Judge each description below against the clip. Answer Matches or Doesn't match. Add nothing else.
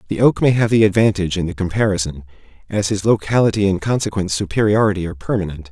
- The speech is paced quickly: Doesn't match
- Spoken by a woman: Doesn't match